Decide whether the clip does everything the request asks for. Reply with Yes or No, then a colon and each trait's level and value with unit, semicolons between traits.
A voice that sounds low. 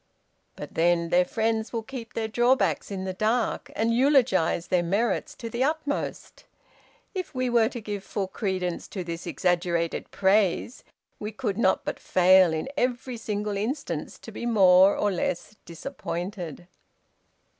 No: high, 210 Hz